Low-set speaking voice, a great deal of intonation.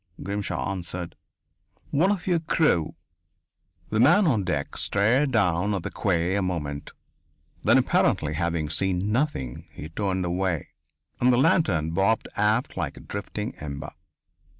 Yes: very low, 95 Hz; wide, 6.1 semitones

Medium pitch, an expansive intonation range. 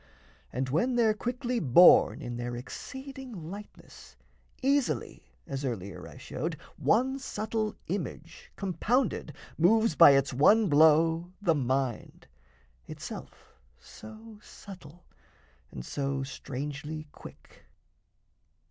Yes: medium, 170 Hz; wide, 8.4 semitones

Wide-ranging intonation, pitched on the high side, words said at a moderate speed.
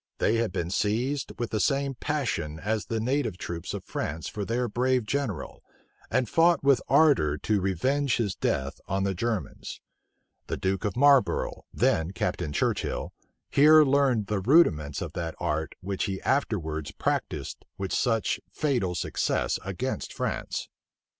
No: wide, 7.0 semitones; low, 110 Hz; average, 150 wpm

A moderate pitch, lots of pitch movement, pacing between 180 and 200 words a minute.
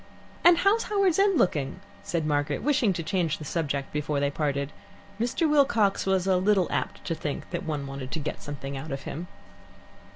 Yes: medium, 160 Hz; wide, 6.8 semitones; average, 185 wpm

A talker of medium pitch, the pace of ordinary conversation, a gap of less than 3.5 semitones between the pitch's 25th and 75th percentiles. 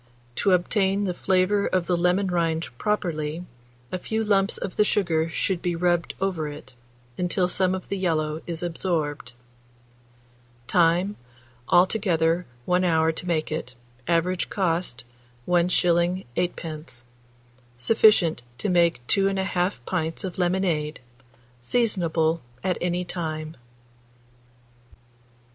No: medium, 175 Hz; slow, 115 wpm; narrow, 2.6 semitones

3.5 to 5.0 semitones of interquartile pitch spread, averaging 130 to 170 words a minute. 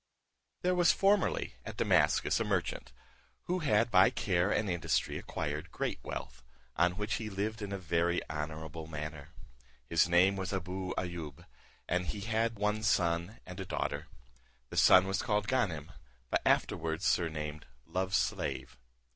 Yes: average, 4.0 semitones; average, 150 wpm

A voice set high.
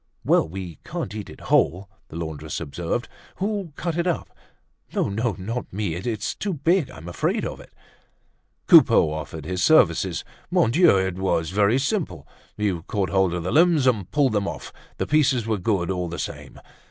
No: low, 100 Hz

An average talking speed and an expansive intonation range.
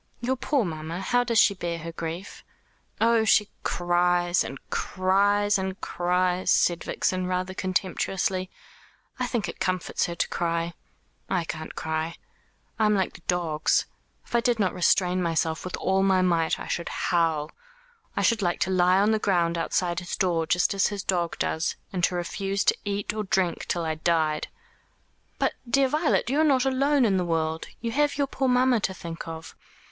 No: average, 185 wpm; average, 3.5 semitones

